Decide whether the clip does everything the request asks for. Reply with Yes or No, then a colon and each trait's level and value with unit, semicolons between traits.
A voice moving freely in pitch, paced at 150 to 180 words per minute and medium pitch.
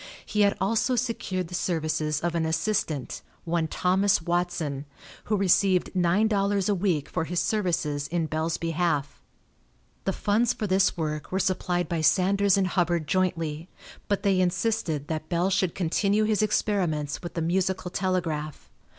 No: average, 3.5 semitones; average, 155 wpm; medium, 180 Hz